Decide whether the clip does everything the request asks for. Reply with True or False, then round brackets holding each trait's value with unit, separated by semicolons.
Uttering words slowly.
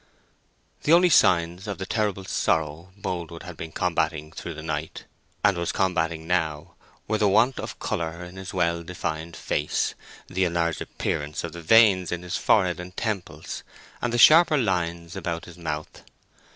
False (165 wpm)